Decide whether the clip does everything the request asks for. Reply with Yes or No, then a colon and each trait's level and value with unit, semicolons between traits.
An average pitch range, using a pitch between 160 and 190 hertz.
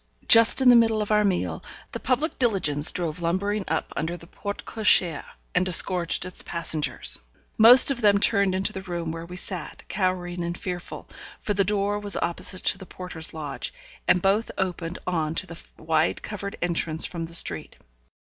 Yes: average, 3.3 semitones; medium, 185 Hz